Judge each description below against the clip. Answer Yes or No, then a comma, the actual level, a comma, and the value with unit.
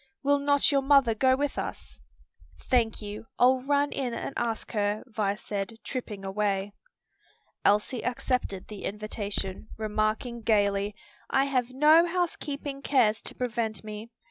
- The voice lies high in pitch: Yes, high, 230 Hz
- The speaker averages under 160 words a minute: Yes, average, 140 wpm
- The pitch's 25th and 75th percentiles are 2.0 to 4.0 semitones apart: No, average, 4.5 semitones